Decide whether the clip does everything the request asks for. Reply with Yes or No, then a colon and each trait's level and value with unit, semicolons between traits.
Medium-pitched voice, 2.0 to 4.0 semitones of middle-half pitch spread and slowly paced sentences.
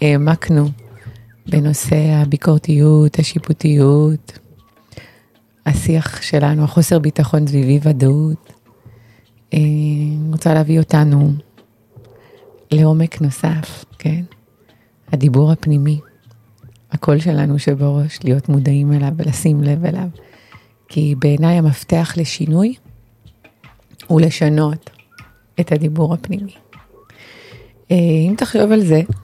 Yes: medium, 150 Hz; narrow, 2.6 semitones; slow, 90 wpm